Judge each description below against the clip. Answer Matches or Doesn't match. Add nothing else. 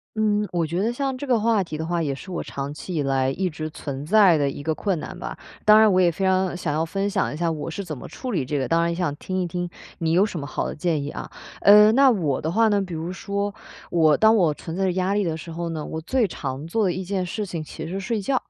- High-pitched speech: Doesn't match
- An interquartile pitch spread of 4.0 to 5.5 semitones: Matches